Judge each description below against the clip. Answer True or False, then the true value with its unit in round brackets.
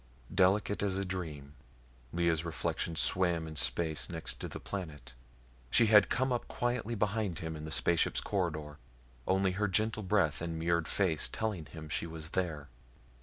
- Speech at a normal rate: True (165 wpm)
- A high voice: False (85 Hz)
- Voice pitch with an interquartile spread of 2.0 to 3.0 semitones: False (4.1 semitones)